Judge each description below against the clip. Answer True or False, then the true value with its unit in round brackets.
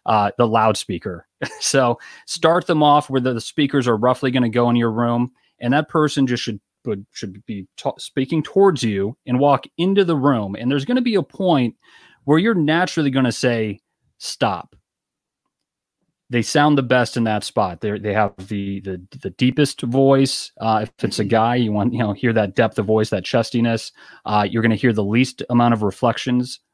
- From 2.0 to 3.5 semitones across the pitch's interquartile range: False (4.6 semitones)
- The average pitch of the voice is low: True (120 Hz)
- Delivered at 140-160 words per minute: False (200 wpm)